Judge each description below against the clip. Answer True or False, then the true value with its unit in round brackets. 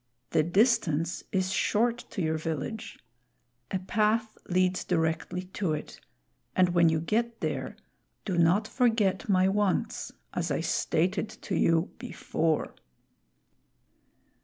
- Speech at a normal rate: False (120 wpm)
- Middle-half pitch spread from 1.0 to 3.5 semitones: False (4.4 semitones)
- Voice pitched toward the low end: False (185 Hz)